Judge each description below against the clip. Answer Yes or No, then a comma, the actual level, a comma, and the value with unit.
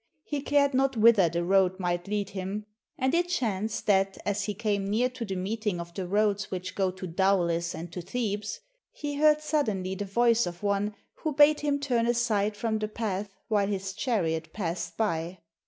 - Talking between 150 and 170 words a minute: No, average, 190 wpm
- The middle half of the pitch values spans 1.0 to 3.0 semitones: No, average, 3.9 semitones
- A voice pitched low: No, high, 205 Hz